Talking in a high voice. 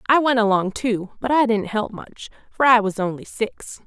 Yes: high, 220 Hz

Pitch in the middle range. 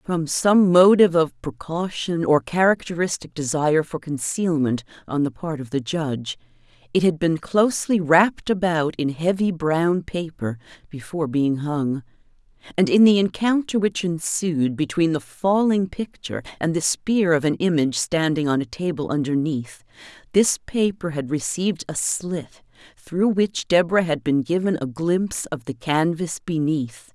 Yes: medium, 165 Hz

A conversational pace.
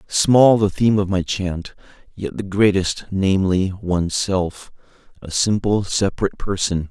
No: slow, 130 wpm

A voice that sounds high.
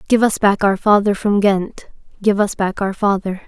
Yes: high, 200 Hz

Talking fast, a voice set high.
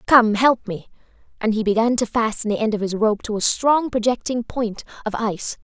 Yes: fast, 210 wpm; high, 225 Hz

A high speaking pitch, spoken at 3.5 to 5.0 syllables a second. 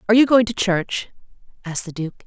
No: high, 205 Hz; 6.9 syllables/s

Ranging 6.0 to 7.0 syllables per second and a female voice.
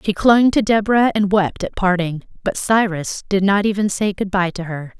No: 5.0 syllables/s; female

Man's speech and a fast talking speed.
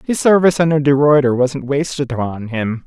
No: male; average, 190 wpm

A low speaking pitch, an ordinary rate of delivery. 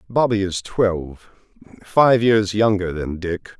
No: low, 100 Hz; slow, 115 wpm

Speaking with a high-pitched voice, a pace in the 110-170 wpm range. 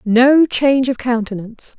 Yes: high, 245 Hz; slow, 135 wpm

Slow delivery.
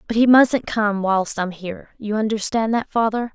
No: average, 195 wpm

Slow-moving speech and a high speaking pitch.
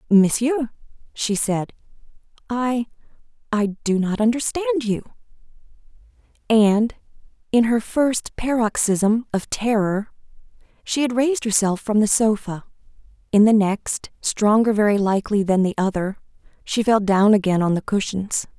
Yes: slow, 125 wpm; high, 215 Hz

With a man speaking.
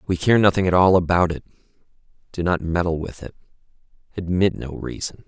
Yes: male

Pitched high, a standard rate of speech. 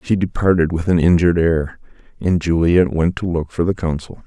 No: very low, 85 Hz; average, 195 wpm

